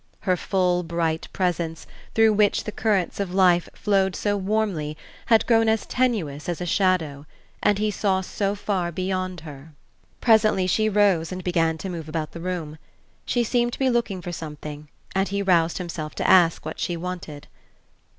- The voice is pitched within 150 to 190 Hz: Yes, medium, 185 Hz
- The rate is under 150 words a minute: No, average, 175 wpm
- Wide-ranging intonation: No, average, 3.8 semitones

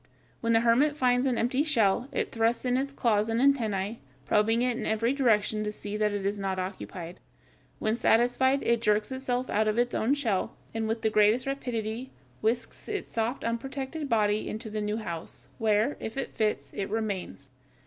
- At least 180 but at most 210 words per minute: Yes, average, 190 wpm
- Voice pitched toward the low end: No, high, 225 Hz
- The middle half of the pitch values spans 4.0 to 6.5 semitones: No, average, 3.0 semitones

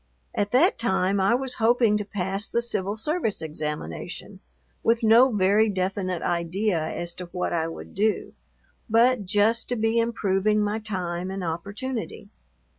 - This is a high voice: Yes, high, 205 Hz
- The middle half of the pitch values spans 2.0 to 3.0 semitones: No, average, 3.6 semitones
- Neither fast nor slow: Yes, average, 150 wpm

